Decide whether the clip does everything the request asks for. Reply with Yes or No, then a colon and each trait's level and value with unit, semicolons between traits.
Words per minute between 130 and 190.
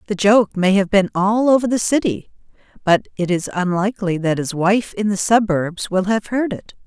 No: average, 200 wpm